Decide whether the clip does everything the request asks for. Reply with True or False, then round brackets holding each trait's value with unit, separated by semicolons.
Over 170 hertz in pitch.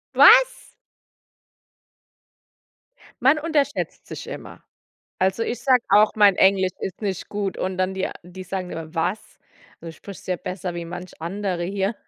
True (190 Hz)